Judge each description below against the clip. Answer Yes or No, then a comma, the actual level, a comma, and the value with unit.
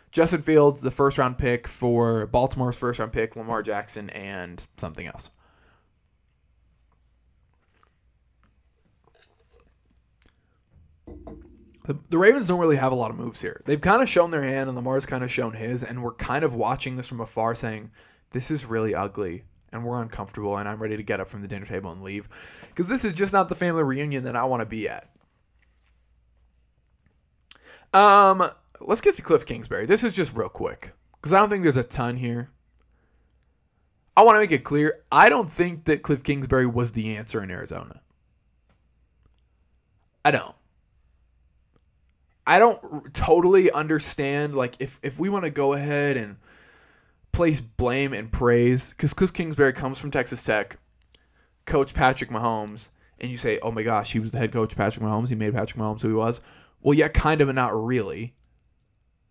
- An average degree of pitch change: No, wide, 6.1 semitones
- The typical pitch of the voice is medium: No, low, 120 Hz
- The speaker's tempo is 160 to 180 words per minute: Yes, average, 175 wpm